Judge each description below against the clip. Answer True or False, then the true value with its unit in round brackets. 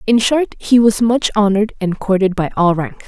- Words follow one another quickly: True (215 wpm)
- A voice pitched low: False (210 Hz)